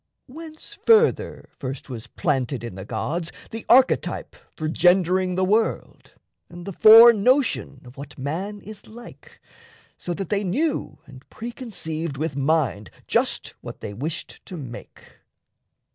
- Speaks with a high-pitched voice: No, medium, 175 Hz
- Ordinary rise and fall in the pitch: No, wide, 7.9 semitones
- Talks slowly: No, average, 145 wpm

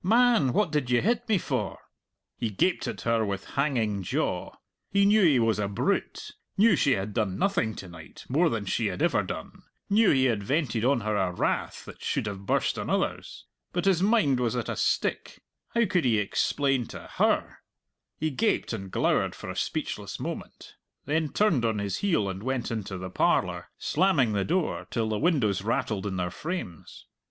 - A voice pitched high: No, low, 125 Hz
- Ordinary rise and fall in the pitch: No, wide, 8.7 semitones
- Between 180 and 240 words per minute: Yes, average, 195 wpm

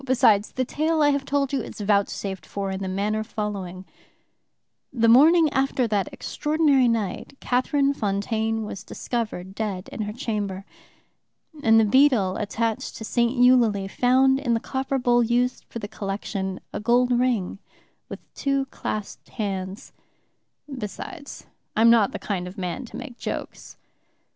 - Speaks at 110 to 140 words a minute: No, average, 150 wpm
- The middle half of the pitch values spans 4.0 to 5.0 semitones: Yes, average, 4.4 semitones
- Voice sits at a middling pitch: No, high, 225 Hz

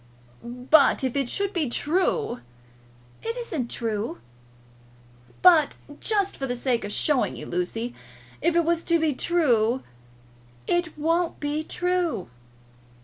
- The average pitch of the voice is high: Yes, very high, 290 Hz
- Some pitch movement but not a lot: No, wide, 6.3 semitones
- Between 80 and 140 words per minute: Yes, slow, 135 wpm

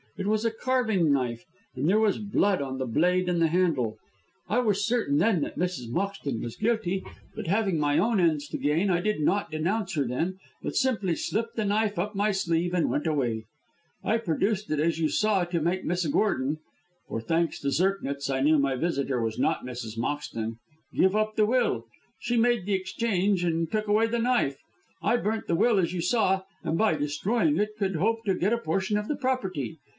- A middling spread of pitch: No, wide, 6.0 semitones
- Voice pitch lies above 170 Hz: Yes, medium, 185 Hz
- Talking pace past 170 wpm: Yes, fast, 205 wpm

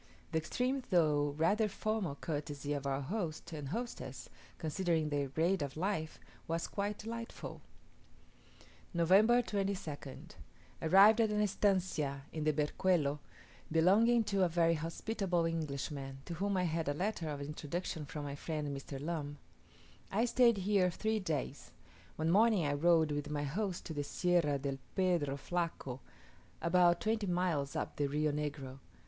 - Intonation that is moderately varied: Yes, average, 4.9 semitones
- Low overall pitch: No, medium, 165 Hz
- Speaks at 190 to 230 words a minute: No, average, 150 wpm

